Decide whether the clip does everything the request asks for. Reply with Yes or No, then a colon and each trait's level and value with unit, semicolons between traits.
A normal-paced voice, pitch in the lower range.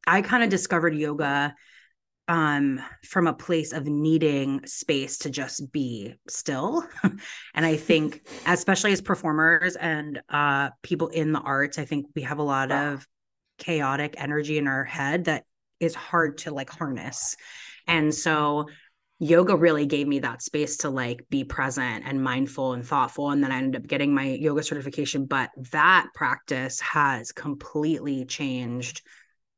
No: average, 155 wpm; medium, 150 Hz